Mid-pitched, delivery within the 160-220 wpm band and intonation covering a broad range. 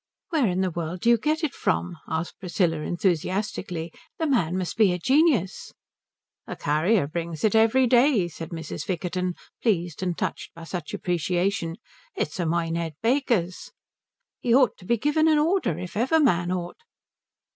Yes: medium, 180 Hz; average, 165 wpm; wide, 5.7 semitones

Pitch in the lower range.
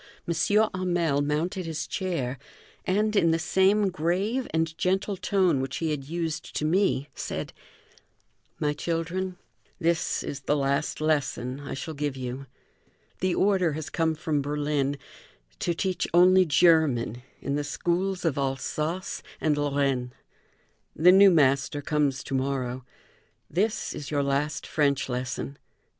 No: medium, 155 Hz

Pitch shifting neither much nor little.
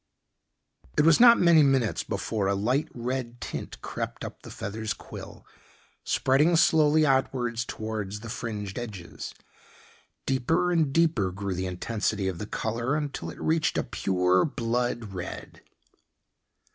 No: wide, 6.1 semitones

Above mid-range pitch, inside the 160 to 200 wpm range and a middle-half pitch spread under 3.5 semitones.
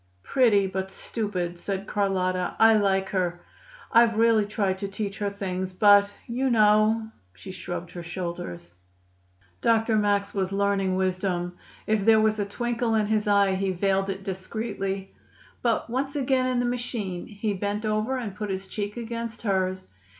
Yes: high, 200 Hz; average, 165 wpm; average, 2.8 semitones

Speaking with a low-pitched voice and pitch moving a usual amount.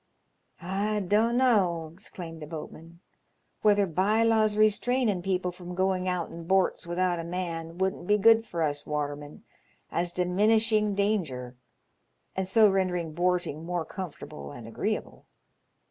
No: medium, 180 Hz; average, 3.8 semitones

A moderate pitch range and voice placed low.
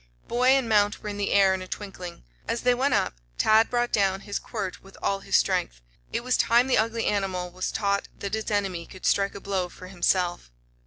No: average, 3.1 semitones; high, 200 Hz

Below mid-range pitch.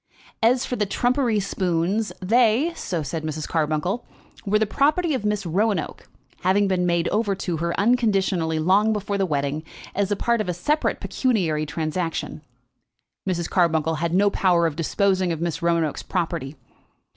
No: medium, 185 Hz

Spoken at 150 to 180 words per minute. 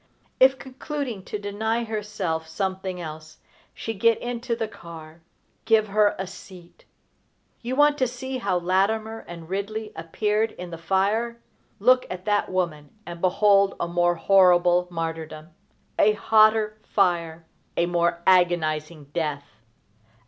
No: slow, 135 wpm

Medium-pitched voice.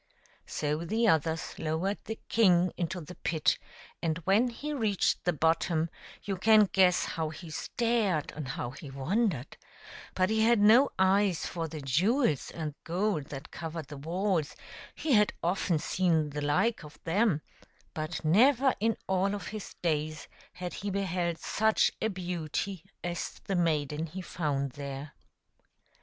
Yes: medium, 175 Hz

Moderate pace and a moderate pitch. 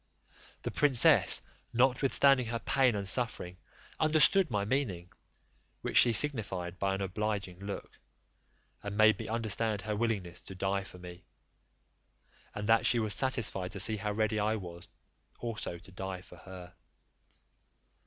No: average, 145 wpm; low, 105 Hz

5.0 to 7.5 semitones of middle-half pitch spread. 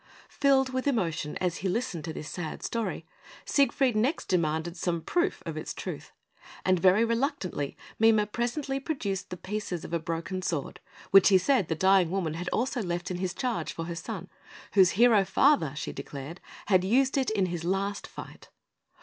Yes: wide, 5.5 semitones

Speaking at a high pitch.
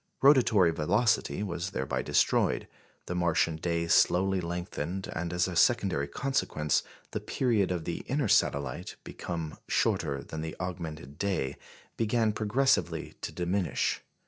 No: very low, 90 Hz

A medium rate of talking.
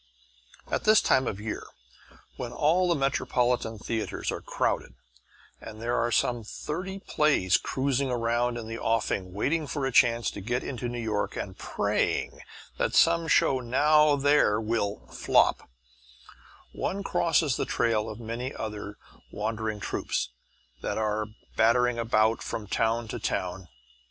Yes: average, 145 wpm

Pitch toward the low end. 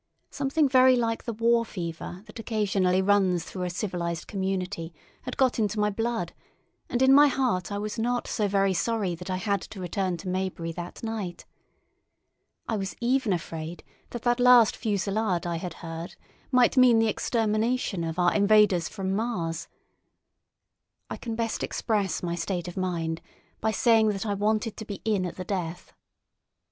No: high, 200 Hz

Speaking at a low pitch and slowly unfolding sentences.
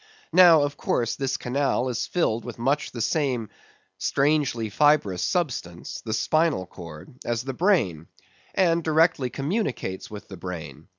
Yes: low, 130 Hz; slow, 130 wpm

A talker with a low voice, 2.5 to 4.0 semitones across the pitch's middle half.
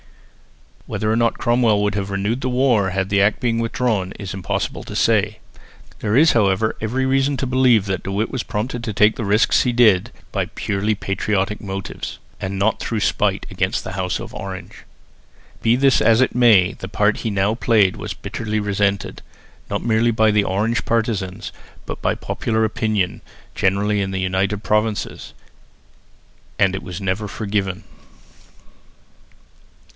Yes: low, 105 Hz; average, 2.9 semitones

